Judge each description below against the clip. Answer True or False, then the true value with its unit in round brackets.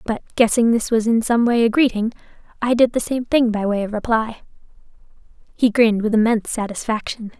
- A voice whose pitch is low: False (225 Hz)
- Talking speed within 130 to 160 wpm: False (185 wpm)